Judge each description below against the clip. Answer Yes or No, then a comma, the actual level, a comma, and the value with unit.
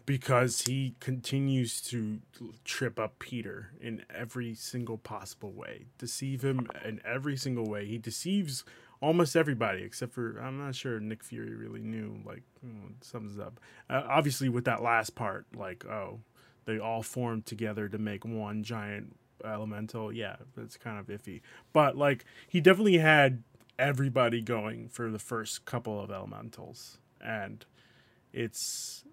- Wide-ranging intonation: No, average, 2.8 semitones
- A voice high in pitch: No, low, 115 Hz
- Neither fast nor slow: Yes, average, 150 wpm